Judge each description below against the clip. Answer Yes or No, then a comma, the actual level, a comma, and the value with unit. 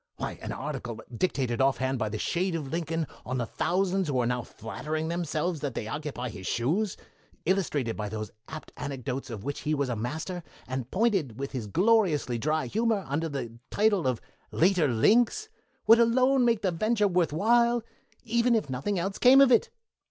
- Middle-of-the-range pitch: Yes, medium, 155 Hz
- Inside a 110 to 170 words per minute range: No, average, 185 wpm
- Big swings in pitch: Yes, wide, 7.8 semitones